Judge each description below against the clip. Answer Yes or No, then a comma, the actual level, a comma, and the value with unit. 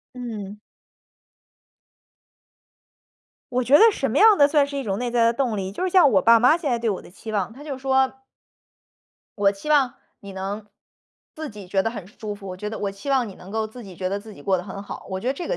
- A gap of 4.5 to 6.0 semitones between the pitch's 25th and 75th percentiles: Yes, average, 5.1 semitones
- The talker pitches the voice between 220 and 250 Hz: Yes, high, 225 Hz